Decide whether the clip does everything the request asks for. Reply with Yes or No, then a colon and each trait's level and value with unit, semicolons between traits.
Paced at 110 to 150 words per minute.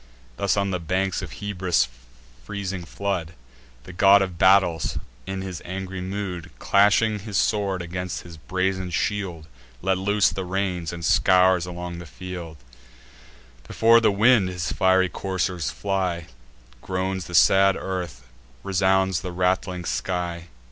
Yes: slow, 135 wpm